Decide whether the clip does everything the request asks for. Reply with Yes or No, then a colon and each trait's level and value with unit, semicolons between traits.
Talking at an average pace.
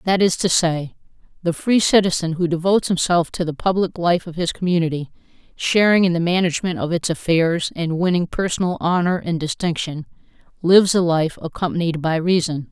Yes: average, 170 wpm